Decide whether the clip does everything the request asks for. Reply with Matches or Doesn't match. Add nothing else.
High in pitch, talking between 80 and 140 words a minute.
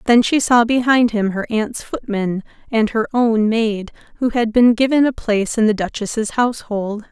Doesn't match